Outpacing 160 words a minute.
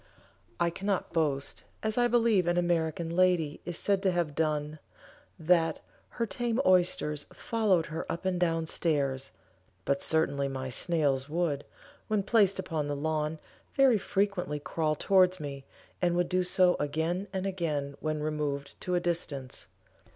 No: average, 150 wpm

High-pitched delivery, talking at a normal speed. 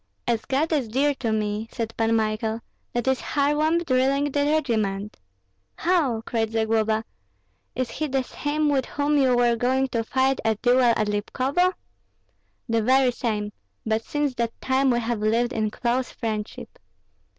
Yes: high, 245 Hz; average, 160 wpm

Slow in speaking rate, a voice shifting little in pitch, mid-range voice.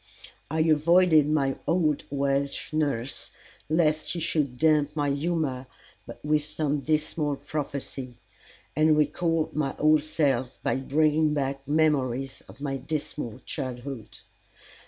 Yes: slow, 115 wpm; narrow, 2.2 semitones; medium, 150 Hz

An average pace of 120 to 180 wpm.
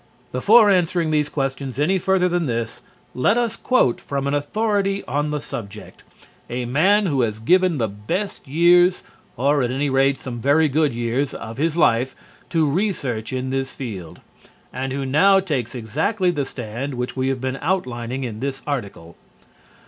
Yes: average, 170 wpm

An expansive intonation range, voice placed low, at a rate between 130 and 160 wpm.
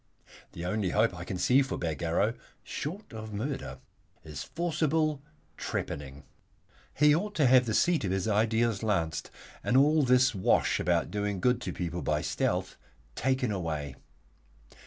Yes: wide, 7.2 semitones; low, 110 Hz; average, 150 wpm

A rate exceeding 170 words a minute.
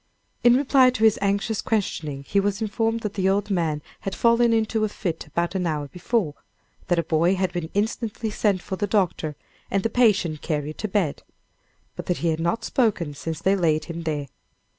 Yes: average, 200 wpm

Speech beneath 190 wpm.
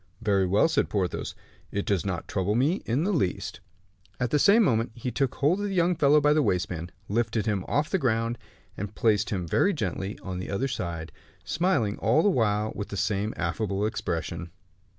No: average, 195 wpm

